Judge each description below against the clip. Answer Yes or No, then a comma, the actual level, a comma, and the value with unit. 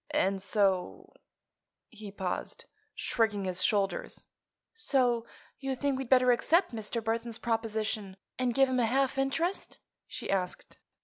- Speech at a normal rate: No, slow, 130 wpm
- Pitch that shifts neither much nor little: Yes, average, 4.5 semitones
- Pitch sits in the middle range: No, high, 230 Hz